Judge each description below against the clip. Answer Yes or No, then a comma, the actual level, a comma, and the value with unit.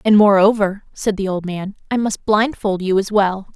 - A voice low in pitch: No, high, 200 Hz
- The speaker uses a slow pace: No, fast, 205 wpm